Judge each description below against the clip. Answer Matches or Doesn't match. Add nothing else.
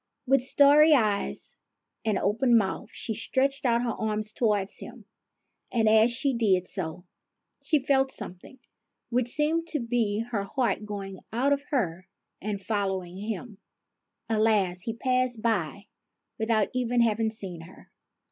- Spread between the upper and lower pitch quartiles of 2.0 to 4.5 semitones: Matches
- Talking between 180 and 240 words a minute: Doesn't match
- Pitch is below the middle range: Doesn't match